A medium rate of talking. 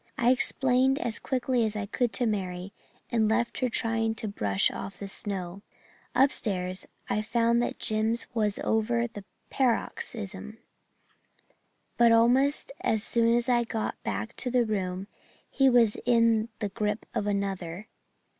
Yes: average, 145 wpm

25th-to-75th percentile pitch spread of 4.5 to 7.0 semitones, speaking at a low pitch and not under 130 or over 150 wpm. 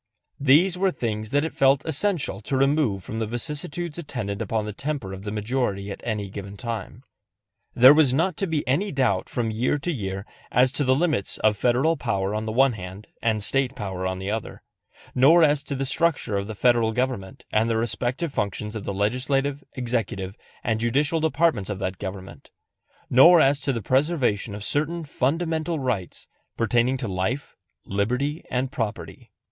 No: wide, 5.6 semitones; low, 125 Hz; average, 180 wpm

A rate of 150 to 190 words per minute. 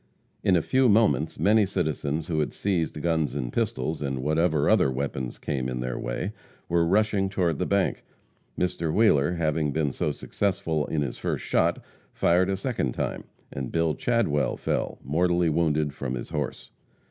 Yes: average, 170 wpm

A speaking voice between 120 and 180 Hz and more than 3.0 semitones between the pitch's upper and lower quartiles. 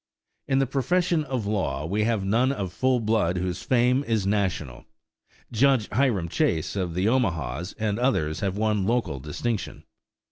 No: low, 105 Hz; wide, 5.4 semitones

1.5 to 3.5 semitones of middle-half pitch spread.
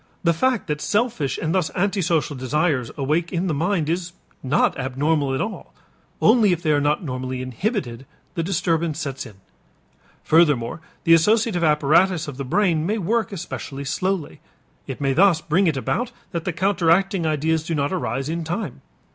No: average, 4.6 semitones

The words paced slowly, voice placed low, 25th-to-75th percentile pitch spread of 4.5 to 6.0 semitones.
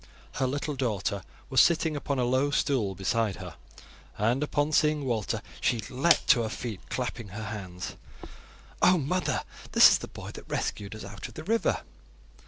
No: average, 175 wpm; low, 125 Hz; wide, 5.4 semitones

